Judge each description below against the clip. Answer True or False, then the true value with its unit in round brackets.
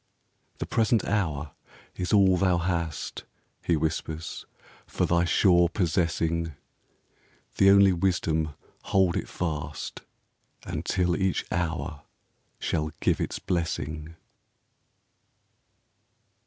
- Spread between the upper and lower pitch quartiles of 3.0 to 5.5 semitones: False (2.6 semitones)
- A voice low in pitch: True (85 Hz)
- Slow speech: True (100 wpm)